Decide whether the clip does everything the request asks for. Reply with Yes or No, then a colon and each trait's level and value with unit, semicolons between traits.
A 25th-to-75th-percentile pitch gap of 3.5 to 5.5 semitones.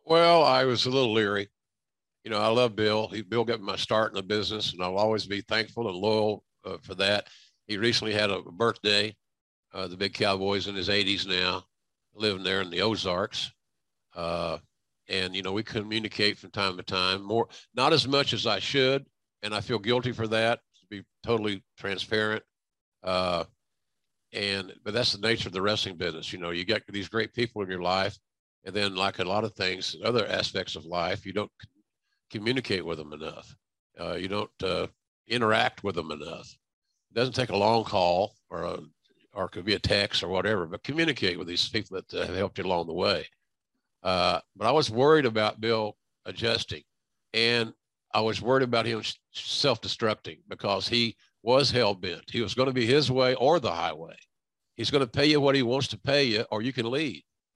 No: average, 3.1 semitones